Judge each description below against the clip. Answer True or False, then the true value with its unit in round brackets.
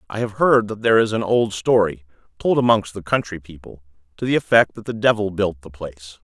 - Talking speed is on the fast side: True (220 wpm)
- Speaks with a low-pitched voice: True (100 Hz)